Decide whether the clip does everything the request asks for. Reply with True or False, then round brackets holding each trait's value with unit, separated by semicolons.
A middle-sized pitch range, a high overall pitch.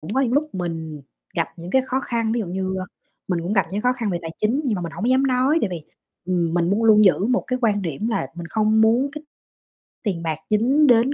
False (6.0 semitones; 215 Hz)